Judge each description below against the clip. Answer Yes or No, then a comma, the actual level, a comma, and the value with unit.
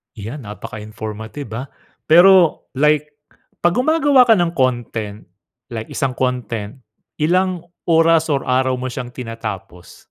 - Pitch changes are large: Yes, wide, 6.8 semitones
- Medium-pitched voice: No, low, 130 Hz